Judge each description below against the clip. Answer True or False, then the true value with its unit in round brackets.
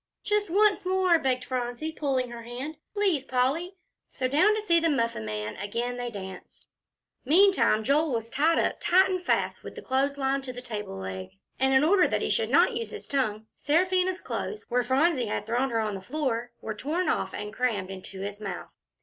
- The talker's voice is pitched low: False (260 Hz)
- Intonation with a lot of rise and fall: True (6.8 semitones)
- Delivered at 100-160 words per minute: False (200 wpm)